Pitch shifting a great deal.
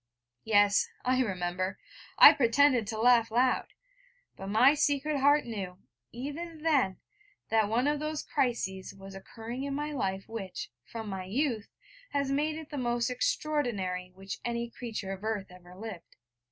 Yes: wide, 6.3 semitones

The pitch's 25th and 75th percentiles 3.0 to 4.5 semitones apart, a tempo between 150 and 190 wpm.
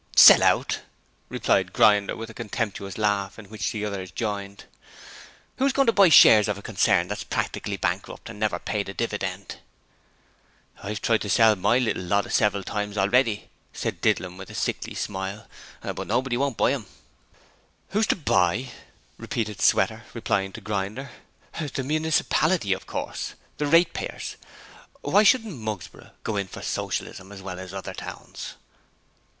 Yes: average, 4.1 semitones; average, 155 wpm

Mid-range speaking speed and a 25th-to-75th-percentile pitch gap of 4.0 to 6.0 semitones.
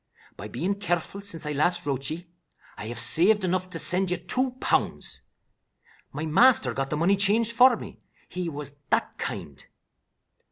Yes: average, 165 wpm; average, 5.1 semitones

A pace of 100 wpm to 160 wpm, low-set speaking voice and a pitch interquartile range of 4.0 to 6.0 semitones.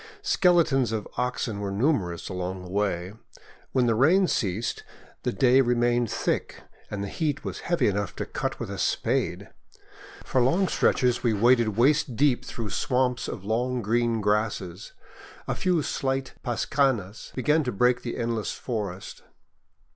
Yes: average, 150 wpm; low, 120 Hz; average, 4.4 semitones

